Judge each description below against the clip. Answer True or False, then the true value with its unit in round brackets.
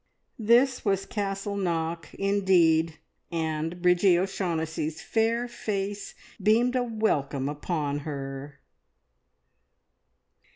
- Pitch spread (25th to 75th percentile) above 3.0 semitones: True (4.4 semitones)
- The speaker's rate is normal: False (85 wpm)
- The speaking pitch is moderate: True (180 Hz)